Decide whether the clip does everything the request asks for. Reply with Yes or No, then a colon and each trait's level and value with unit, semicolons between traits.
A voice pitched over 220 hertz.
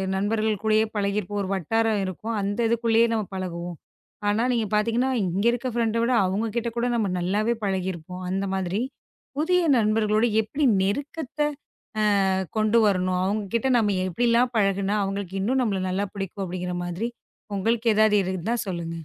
No: high, 210 Hz